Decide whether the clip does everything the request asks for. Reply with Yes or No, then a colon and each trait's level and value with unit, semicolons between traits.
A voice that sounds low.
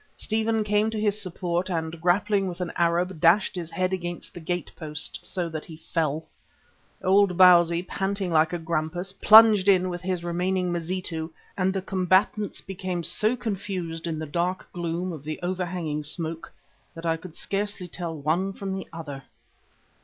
No: medium, 180 Hz